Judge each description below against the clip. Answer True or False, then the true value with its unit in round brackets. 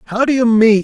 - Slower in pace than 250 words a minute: False (290 wpm)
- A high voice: True (225 Hz)